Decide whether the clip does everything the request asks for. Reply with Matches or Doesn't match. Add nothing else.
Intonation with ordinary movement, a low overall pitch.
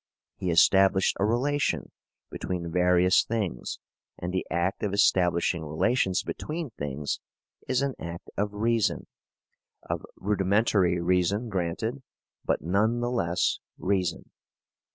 Matches